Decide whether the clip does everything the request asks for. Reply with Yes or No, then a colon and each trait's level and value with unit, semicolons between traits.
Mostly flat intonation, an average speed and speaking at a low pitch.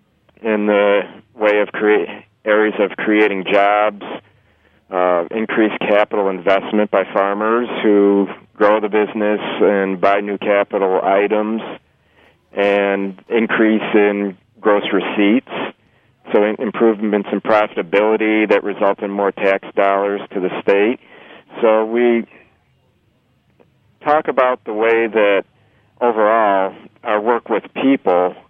No: narrow, 1.6 semitones; slow, 115 wpm; low, 105 Hz